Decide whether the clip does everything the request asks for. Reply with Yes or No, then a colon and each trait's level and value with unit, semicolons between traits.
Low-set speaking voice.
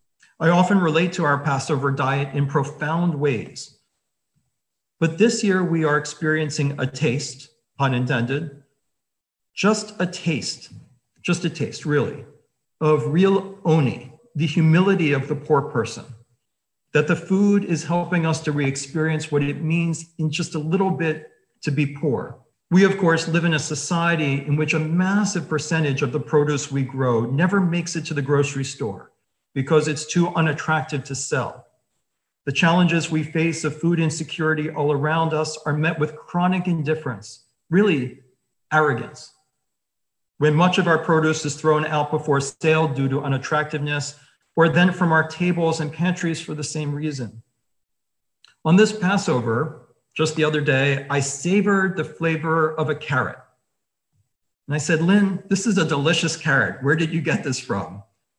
No: medium, 155 Hz